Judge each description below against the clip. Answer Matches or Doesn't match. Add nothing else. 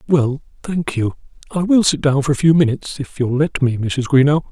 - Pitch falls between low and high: Matches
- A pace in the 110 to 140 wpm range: Doesn't match